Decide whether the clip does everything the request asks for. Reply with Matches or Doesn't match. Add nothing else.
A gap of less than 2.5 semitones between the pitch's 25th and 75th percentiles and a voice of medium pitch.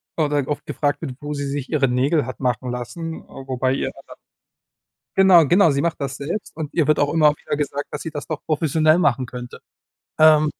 Doesn't match